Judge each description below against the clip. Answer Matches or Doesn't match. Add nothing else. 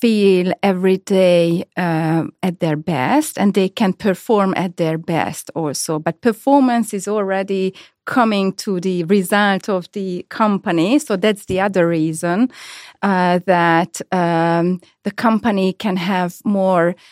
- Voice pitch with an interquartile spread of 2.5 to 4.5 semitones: Matches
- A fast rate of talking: Doesn't match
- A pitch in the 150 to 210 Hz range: Matches